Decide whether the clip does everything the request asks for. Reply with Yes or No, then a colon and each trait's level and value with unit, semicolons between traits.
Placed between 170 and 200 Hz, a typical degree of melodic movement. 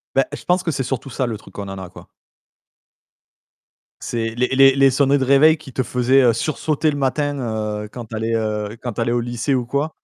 No: low, 130 Hz; average, 3.3 semitones